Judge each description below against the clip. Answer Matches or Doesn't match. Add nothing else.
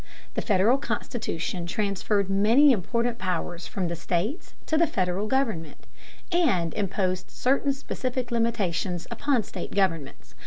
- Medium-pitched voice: Doesn't match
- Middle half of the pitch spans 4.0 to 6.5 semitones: Matches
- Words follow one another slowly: Matches